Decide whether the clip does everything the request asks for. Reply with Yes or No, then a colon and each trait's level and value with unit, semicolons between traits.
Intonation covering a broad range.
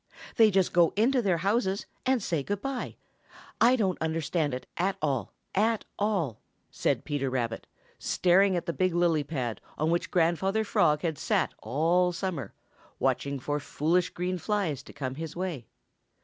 No: average, 4.7 semitones